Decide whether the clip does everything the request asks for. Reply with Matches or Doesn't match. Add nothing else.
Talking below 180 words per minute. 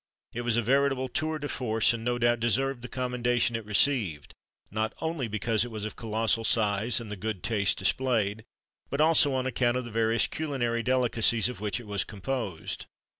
Doesn't match